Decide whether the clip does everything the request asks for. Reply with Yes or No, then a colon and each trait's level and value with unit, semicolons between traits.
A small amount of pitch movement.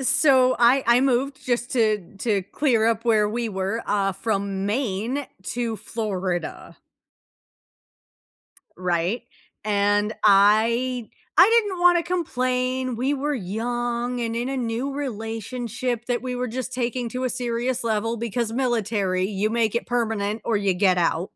No: average, 3.4 semitones